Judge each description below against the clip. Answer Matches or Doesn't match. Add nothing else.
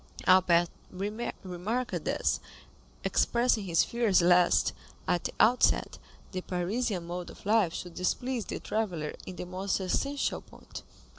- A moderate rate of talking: Doesn't match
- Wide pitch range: Doesn't match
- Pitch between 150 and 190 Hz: Matches